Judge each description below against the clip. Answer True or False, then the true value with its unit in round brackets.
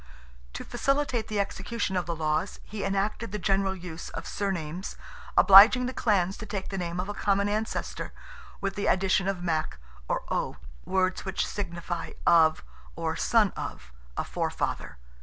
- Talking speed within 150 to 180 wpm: True (160 wpm)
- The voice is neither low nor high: False (195 Hz)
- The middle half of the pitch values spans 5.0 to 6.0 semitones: False (2.9 semitones)